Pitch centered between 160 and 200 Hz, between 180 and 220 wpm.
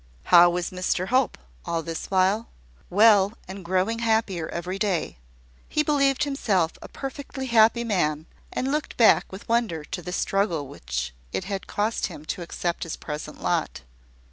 No: high, 190 Hz; average, 160 wpm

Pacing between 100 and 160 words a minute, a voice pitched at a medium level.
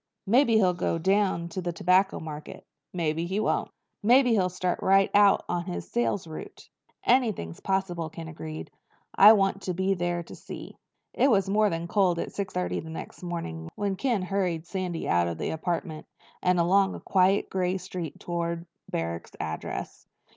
No: average, 175 wpm; medium, 180 Hz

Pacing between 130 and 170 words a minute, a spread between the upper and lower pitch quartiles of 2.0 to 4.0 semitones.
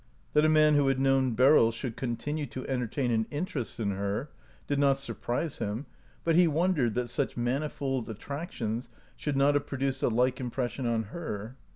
No: average, 190 wpm; average, 3.5 semitones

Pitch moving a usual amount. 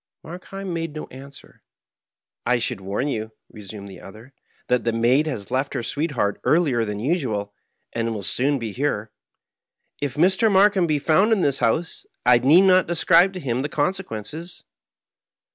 No: wide, 6.9 semitones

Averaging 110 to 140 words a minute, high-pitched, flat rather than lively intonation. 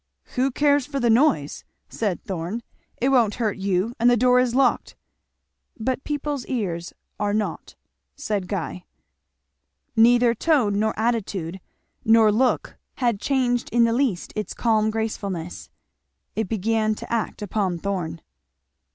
No: slow, 135 wpm; high, 225 Hz; average, 3.6 semitones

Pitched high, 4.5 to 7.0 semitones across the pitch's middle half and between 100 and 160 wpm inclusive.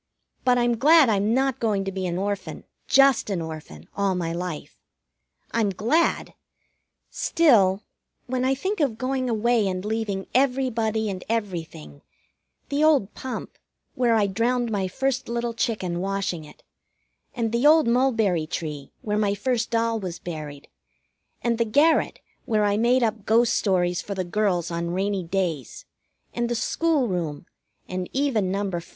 Yes: high, 215 Hz; average, 4.8 semitones; average, 155 wpm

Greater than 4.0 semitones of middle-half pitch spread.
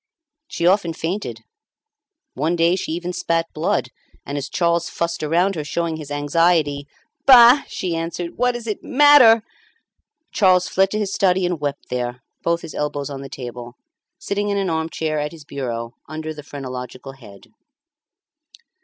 Yes: average, 4.5 semitones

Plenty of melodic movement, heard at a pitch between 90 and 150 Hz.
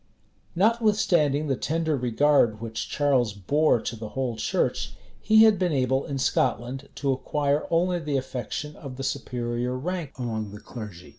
No: average, 4.4 semitones; low, 135 Hz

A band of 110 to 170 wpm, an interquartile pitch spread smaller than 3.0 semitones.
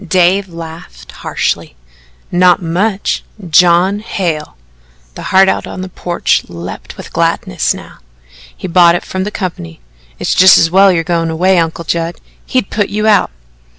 Yes: average, 155 wpm; narrow, 2.4 semitones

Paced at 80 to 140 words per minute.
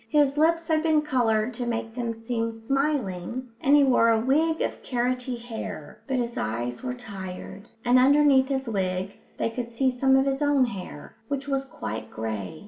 No: average, 185 wpm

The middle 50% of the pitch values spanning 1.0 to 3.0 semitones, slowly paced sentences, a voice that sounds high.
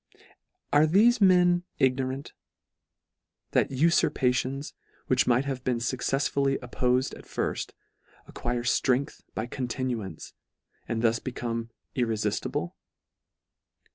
No: average, 2.7 semitones; slow, 95 wpm; low, 130 Hz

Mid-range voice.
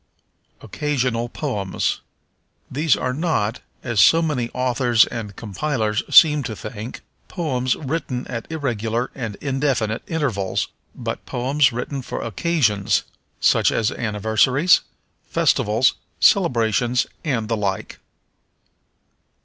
No: low, 125 Hz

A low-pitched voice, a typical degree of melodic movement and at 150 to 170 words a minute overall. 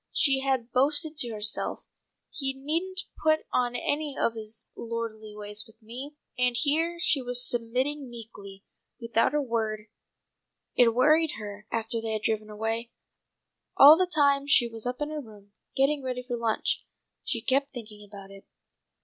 No: high, 245 Hz; average, 4.3 semitones; average, 160 wpm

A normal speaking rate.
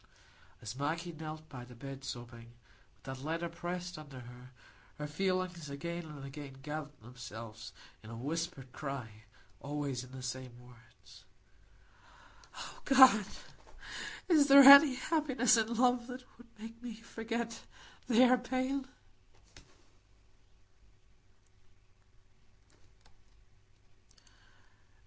No: slow, 105 wpm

